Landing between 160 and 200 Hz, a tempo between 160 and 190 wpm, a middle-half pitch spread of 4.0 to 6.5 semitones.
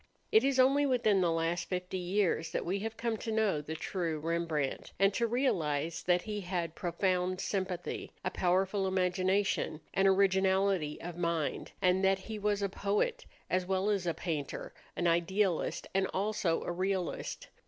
No: medium, 185 Hz; average, 165 wpm; average, 2.8 semitones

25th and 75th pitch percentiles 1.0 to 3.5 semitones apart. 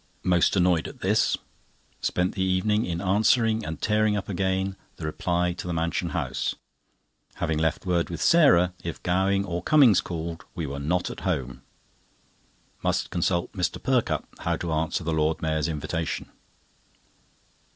Yes: average, 2.8 semitones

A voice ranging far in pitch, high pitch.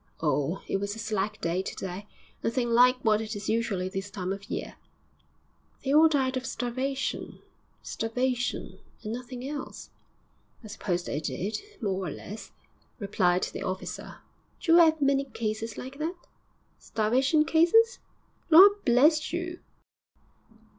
Yes: wide, 5.7 semitones; high, 230 Hz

